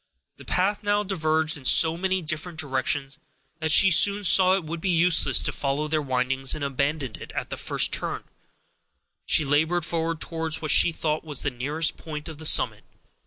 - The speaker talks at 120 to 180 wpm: No, average, 190 wpm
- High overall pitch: No, medium, 160 Hz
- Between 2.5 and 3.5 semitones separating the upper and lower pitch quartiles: Yes, average, 2.8 semitones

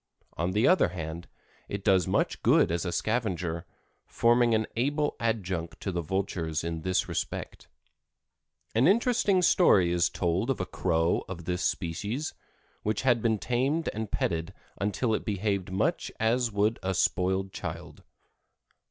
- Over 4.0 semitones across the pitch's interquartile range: Yes, average, 5.0 semitones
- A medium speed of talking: Yes, average, 150 wpm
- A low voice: Yes, low, 100 Hz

